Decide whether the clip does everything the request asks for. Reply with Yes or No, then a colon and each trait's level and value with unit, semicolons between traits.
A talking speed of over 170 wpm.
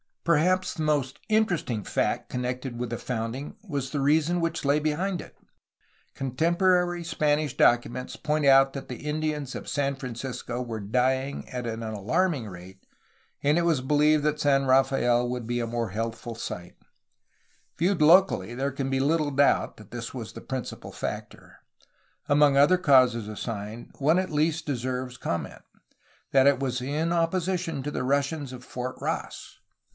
No: average, 160 wpm